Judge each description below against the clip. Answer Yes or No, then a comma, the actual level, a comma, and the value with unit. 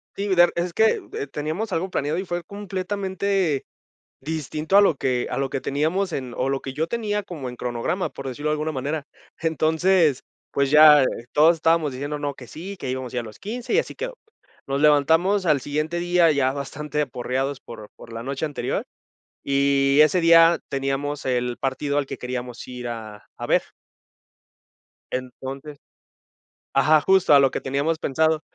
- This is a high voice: No, medium, 150 Hz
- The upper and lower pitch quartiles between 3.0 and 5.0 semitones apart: Yes, average, 4.2 semitones